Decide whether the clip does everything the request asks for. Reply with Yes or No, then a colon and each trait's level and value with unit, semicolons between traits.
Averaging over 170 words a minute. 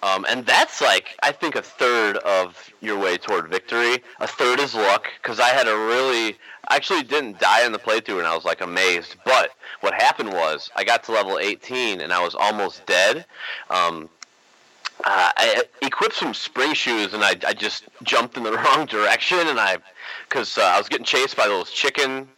Yes: fast, 205 wpm